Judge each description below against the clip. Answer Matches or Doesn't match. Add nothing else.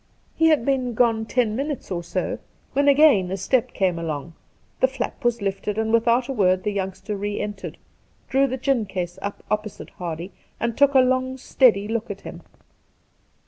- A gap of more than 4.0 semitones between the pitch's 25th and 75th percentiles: Matches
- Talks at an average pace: Matches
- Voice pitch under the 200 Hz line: Doesn't match